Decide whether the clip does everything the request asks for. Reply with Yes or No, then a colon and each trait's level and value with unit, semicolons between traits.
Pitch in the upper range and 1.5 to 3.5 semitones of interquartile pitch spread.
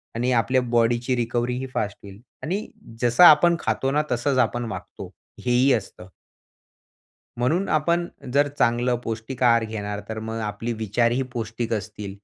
No: low, 120 Hz; narrow, 2.5 semitones